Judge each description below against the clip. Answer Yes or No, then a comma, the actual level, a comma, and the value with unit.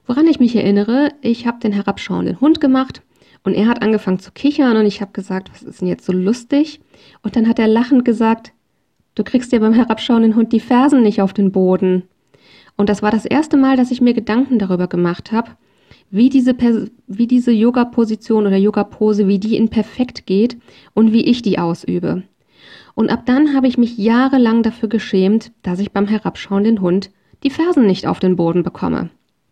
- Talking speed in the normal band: No, fast, 195 wpm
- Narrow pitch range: No, average, 3.5 semitones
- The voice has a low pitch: No, high, 225 Hz